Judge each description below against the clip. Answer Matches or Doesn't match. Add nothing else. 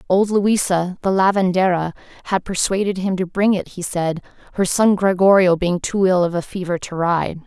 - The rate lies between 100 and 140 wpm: Doesn't match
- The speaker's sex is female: Matches